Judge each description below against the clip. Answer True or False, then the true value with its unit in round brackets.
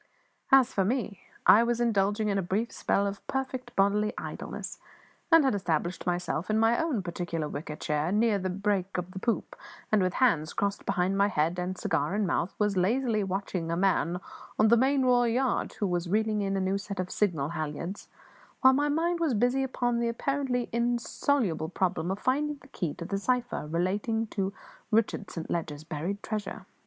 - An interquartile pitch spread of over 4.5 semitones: True (4.9 semitones)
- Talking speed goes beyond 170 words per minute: True (190 wpm)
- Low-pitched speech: False (200 Hz)